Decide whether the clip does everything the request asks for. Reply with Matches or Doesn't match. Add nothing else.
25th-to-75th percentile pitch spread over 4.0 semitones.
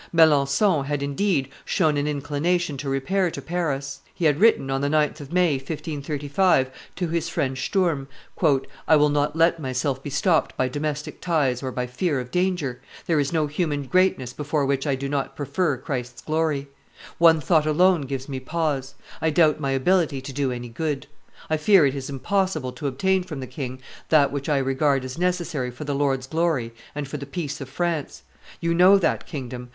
Doesn't match